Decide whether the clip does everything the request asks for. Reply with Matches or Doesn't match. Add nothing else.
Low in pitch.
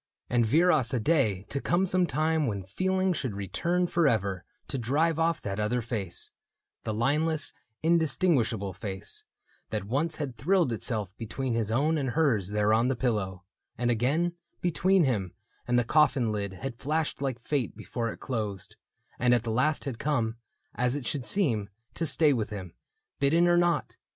Matches